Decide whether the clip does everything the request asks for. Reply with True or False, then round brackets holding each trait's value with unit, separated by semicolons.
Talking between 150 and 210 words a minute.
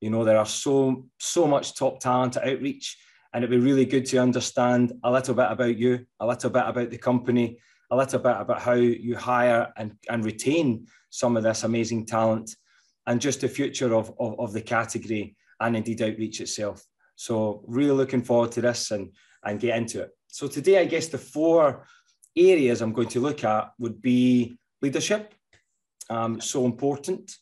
True (185 wpm)